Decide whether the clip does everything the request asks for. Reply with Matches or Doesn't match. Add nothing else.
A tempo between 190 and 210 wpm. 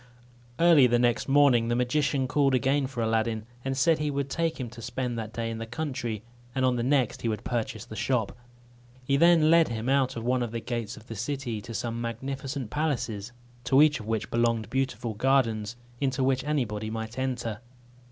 Matches